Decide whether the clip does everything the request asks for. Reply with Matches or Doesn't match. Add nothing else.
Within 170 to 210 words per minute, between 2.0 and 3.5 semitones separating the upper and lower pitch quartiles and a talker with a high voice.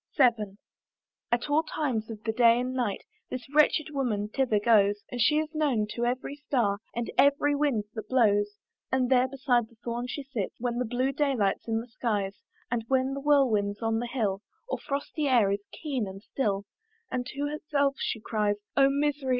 Doesn't match